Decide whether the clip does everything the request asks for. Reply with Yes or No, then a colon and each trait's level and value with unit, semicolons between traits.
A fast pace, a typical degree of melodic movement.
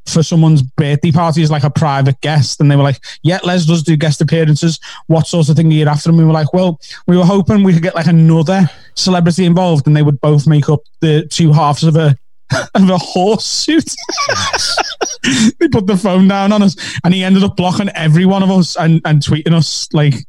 Yes: fast, 230 wpm; average, 3.3 semitones